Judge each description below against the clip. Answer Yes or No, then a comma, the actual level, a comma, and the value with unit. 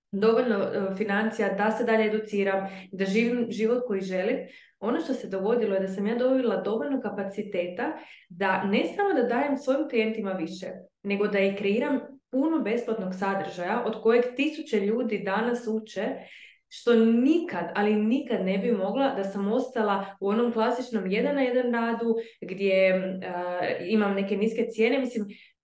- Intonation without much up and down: No, average, 3.4 semitones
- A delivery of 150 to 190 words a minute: Yes, average, 155 wpm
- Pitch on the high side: Yes, high, 220 Hz